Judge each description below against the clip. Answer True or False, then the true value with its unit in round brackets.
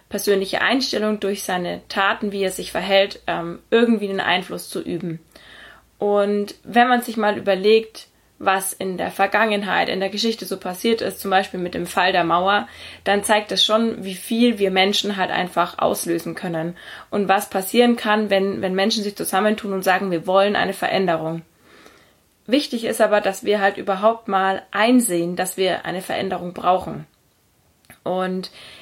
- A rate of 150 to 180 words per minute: True (165 wpm)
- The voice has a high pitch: True (195 Hz)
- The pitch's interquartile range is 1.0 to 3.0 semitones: True (2.4 semitones)